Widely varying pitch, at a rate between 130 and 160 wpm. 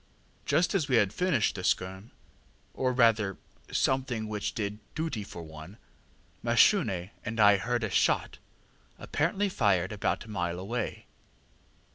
No: average, 4.8 semitones; slow, 135 wpm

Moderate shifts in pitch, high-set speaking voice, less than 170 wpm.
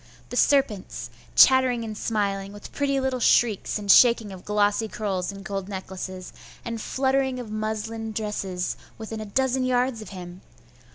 Yes: average, 3.8 semitones; high, 215 Hz; average, 155 wpm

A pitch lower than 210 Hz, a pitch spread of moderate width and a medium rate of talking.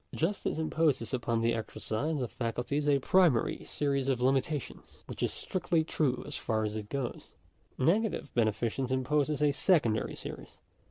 Yes: low, 135 Hz; average, 4.6 semitones; average, 150 wpm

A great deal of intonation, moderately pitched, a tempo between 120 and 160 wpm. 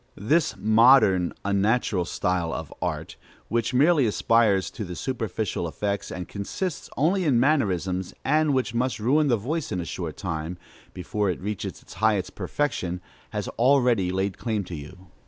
No: wide, 5.9 semitones; low, 105 Hz; average, 155 wpm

